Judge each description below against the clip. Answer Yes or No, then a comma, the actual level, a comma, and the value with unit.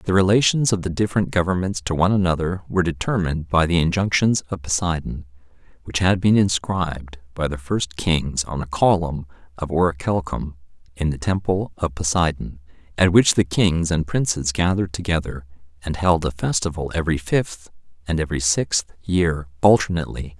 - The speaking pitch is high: No, very low, 85 Hz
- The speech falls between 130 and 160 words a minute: Yes, average, 155 wpm